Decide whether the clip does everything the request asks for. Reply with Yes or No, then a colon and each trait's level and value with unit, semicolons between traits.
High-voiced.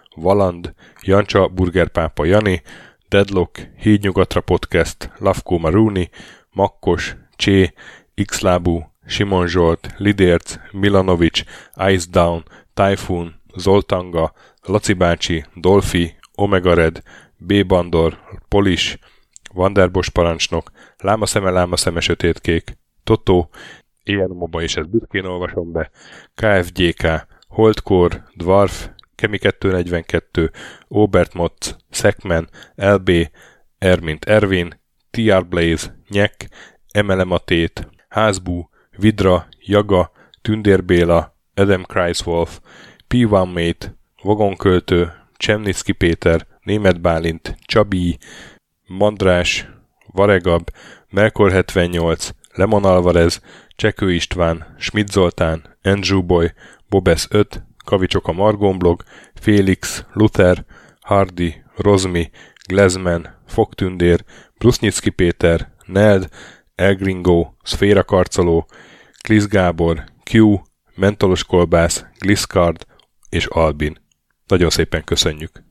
No: very low, 90 Hz